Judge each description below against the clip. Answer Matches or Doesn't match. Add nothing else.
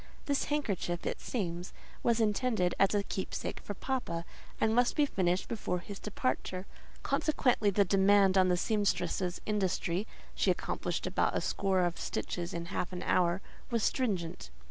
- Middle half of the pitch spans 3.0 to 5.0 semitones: Matches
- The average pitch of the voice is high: Matches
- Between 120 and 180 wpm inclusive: Matches